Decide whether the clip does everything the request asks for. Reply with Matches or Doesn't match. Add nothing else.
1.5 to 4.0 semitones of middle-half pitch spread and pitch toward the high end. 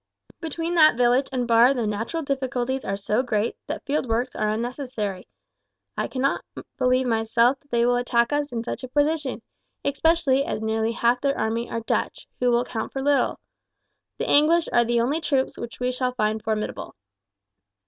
Matches